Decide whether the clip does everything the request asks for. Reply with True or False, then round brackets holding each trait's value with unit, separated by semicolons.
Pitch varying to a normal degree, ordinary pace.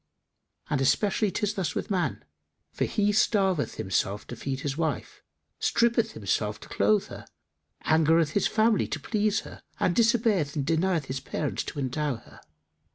False (7.3 semitones; 160 wpm)